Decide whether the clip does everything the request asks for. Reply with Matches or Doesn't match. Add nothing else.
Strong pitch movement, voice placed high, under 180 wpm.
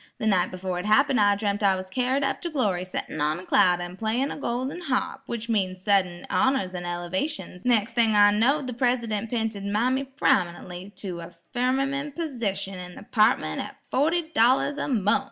Doesn't match